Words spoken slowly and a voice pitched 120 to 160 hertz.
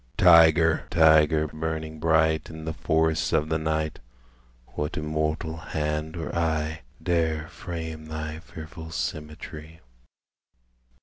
No: slow, 110 wpm; very low, 80 Hz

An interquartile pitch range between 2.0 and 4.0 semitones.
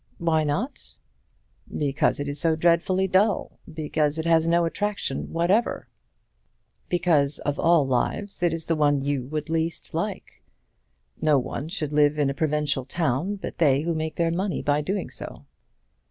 Yes: average, 2.8 semitones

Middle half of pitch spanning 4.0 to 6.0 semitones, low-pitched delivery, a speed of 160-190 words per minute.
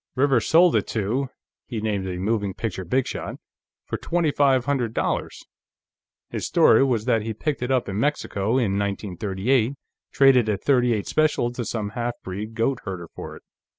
Yes: average, 4.4 semitones; low, 115 Hz; average, 165 wpm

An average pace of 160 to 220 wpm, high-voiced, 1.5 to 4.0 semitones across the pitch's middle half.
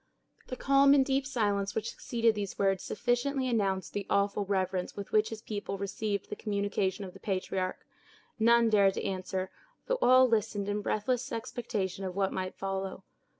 Yes: average, 170 wpm; high, 205 Hz; average, 3.1 semitones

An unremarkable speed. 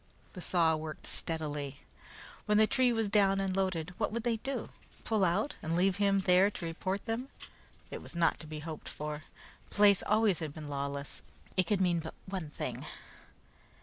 Yes: average, 185 wpm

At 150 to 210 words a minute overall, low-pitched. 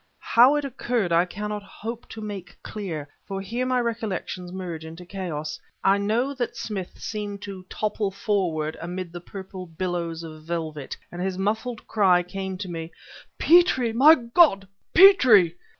No: average, 160 wpm; high, 195 Hz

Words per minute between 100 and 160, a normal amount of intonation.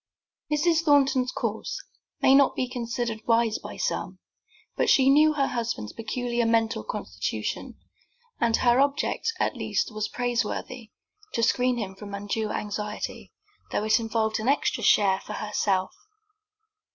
Yes: average, 140 wpm; average, 3.3 semitones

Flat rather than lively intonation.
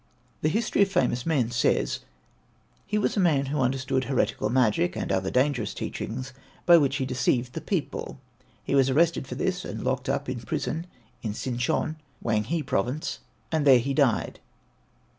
No: average, 4.2 semitones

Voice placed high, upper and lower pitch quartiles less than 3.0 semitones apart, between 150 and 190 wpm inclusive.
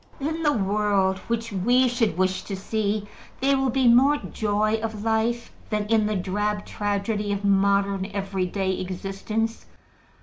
Yes: high, 210 Hz; narrow, 2.5 semitones; average, 155 wpm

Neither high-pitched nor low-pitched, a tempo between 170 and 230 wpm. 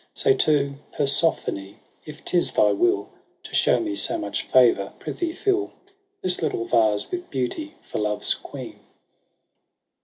No: medium, 150 Hz; slow, 135 wpm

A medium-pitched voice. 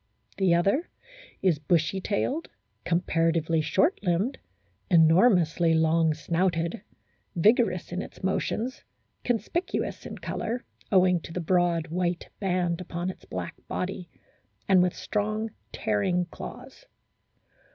Yes: medium, 180 Hz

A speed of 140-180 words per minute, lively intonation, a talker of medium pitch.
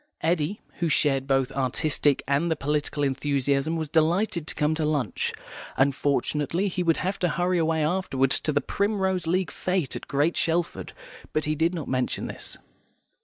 No: average, 170 wpm; average, 3.6 semitones; medium, 155 Hz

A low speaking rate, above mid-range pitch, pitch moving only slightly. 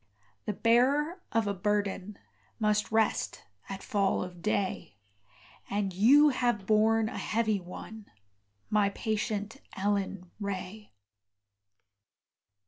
Yes: slow, 105 wpm; high, 210 Hz; narrow, 2.1 semitones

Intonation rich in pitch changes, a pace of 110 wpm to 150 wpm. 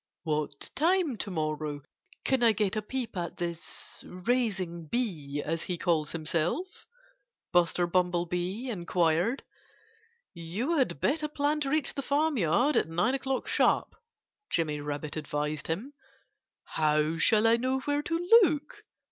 Yes: wide, 8.5 semitones; slow, 135 wpm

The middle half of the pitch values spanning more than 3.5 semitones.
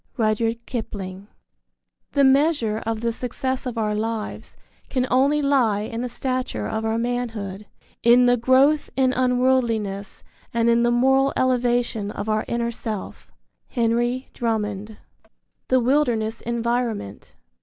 No: average, 2.7 semitones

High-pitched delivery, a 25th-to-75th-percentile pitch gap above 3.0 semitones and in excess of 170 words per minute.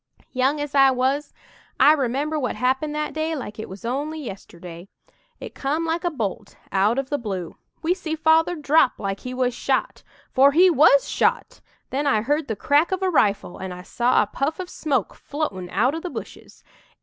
Yes: very high, 275 Hz; wide, 5.5 semitones; average, 195 wpm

